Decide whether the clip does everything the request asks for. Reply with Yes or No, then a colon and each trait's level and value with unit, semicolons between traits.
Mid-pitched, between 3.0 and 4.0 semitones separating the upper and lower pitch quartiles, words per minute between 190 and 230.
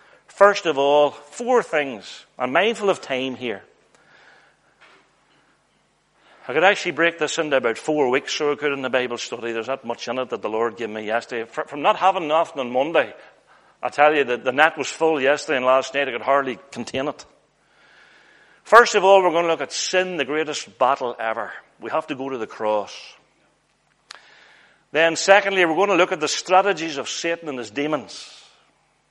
No: medium, 150 Hz; average, 4.6 semitones; average, 195 wpm